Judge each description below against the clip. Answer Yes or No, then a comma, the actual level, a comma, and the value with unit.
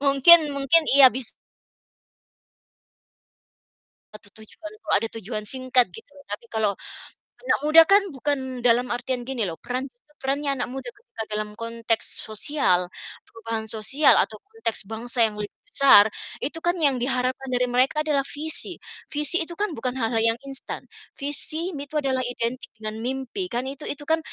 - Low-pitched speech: No, very high, 260 Hz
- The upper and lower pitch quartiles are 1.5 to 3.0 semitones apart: No, average, 4.3 semitones